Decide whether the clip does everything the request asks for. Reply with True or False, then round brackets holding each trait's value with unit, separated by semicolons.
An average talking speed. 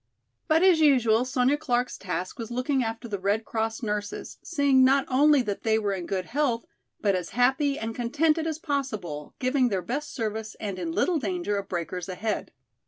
True (185 wpm)